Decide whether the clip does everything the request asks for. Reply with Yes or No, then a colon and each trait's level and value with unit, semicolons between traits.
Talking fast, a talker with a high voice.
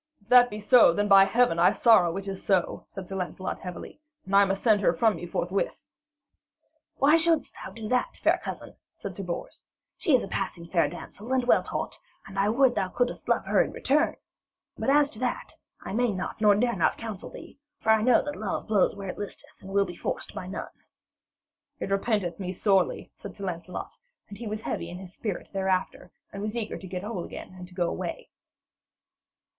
Yes: fast, 215 wpm; high, 200 Hz